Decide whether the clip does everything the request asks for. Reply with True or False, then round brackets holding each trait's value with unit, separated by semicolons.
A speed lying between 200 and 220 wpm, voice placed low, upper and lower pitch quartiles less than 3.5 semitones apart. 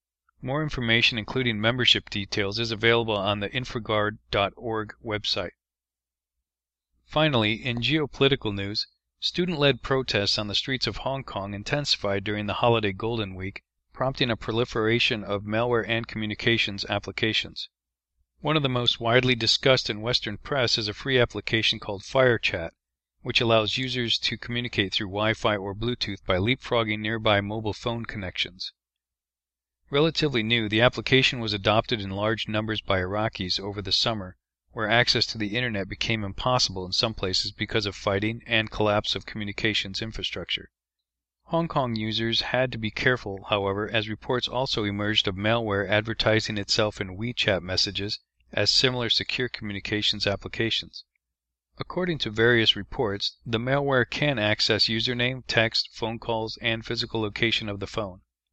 False (145 wpm; 110 Hz; 3.0 semitones)